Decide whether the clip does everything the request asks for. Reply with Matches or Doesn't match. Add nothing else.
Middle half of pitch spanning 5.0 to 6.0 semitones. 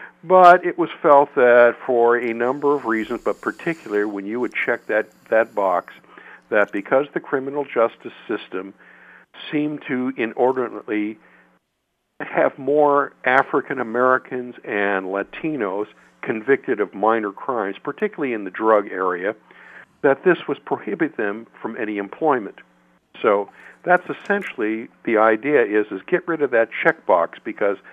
Matches